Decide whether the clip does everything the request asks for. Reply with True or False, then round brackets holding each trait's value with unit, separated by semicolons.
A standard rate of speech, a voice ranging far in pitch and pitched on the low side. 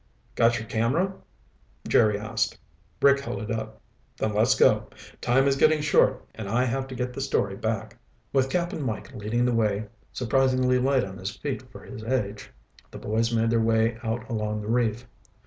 False (180 wpm; 3.2 semitones; 115 Hz)